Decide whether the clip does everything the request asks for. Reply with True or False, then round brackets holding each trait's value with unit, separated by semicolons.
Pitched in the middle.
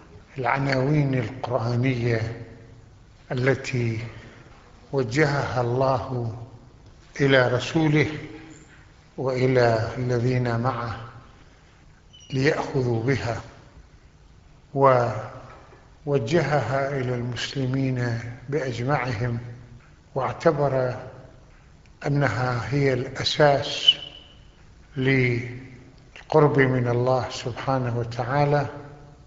False (130 Hz)